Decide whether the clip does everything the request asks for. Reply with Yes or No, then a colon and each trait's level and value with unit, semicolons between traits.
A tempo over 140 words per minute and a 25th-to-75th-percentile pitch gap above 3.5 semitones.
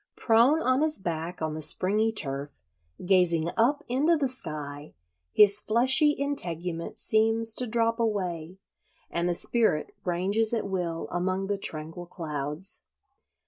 No: slow, 135 wpm; wide, 5.6 semitones